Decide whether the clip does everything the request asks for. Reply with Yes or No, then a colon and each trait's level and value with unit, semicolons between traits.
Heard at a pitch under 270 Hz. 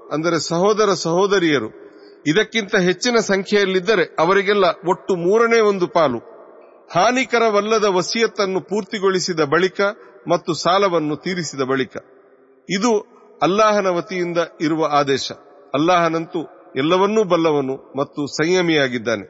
Yes: medium, 185 Hz